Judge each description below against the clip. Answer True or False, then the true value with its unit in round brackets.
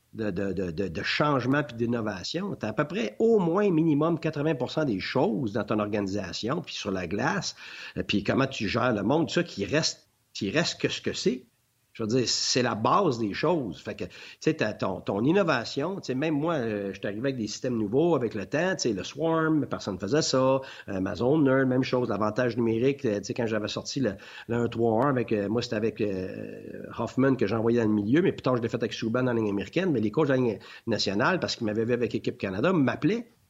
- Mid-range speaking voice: False (120 Hz)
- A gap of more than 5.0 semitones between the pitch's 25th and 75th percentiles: True (5.6 semitones)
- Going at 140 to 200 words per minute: False (220 wpm)